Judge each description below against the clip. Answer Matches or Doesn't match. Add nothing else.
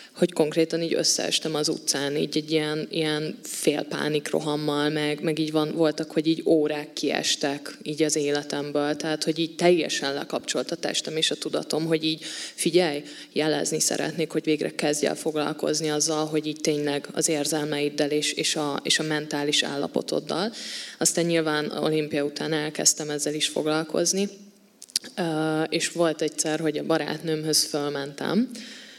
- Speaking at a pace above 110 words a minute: Matches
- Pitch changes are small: Matches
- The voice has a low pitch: Doesn't match